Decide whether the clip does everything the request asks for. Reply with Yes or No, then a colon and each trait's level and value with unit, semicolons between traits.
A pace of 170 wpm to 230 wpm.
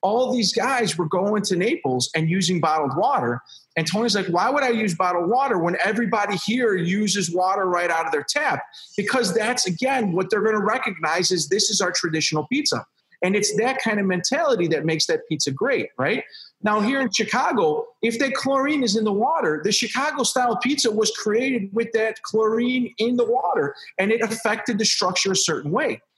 Yes: average, 200 wpm